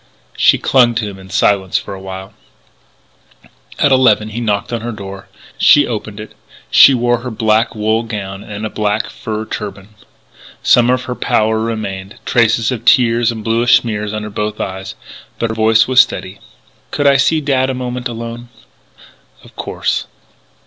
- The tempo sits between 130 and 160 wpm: No, average, 170 wpm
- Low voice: Yes, low, 110 Hz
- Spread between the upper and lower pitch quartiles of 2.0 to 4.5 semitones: Yes, narrow, 2.5 semitones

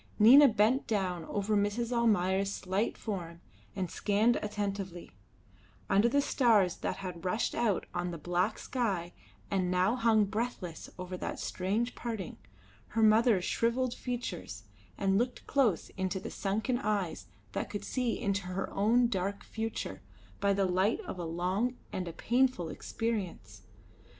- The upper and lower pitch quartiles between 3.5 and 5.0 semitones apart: Yes, average, 4.1 semitones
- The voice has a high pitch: Yes, high, 200 Hz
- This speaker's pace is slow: No, average, 145 wpm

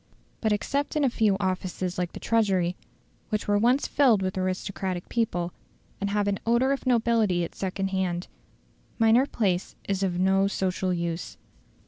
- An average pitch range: Yes, average, 3.6 semitones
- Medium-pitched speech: No, high, 195 Hz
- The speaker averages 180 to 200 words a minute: No, average, 160 wpm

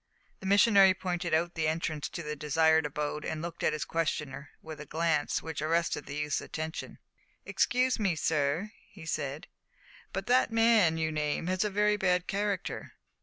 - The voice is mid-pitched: Yes, medium, 165 Hz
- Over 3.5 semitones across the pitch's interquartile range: Yes, average, 4.0 semitones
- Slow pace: No, average, 170 wpm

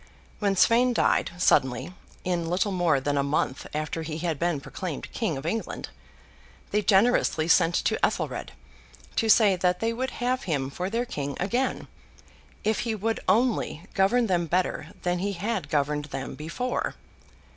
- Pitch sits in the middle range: Yes, medium, 180 Hz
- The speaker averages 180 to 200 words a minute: No, average, 160 wpm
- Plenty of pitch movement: Yes, wide, 6.3 semitones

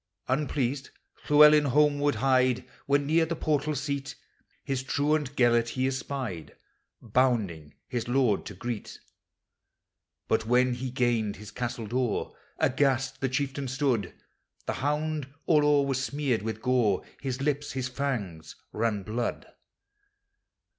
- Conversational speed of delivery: No, slow, 125 wpm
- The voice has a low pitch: Yes, low, 130 Hz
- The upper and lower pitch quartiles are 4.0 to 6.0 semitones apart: No, average, 3.2 semitones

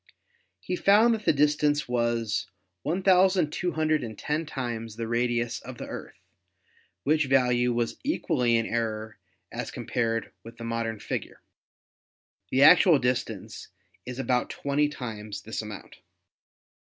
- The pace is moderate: No, slow, 120 wpm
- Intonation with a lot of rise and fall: No, average, 4.6 semitones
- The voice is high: No, low, 125 Hz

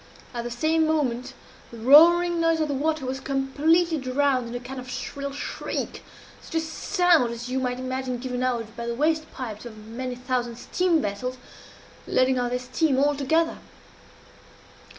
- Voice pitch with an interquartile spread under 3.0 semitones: No, average, 4.1 semitones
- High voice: Yes, very high, 260 Hz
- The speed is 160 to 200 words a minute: Yes, average, 170 wpm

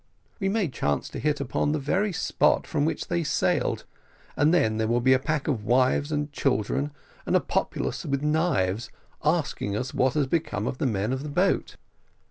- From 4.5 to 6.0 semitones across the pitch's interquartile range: No, average, 4.1 semitones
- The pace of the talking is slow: No, average, 195 wpm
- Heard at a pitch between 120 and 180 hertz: Yes, medium, 140 Hz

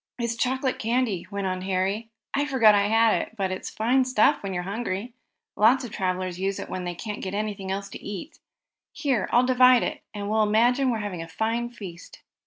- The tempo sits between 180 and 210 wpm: Yes, fast, 205 wpm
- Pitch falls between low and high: No, high, 215 Hz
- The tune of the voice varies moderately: Yes, average, 4.0 semitones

